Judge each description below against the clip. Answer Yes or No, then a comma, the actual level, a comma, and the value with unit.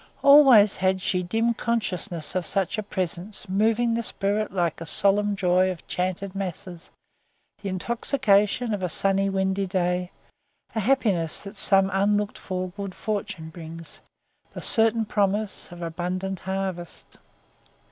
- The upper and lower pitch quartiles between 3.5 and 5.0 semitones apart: No, narrow, 2.5 semitones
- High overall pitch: Yes, high, 195 Hz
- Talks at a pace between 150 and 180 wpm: No, slow, 135 wpm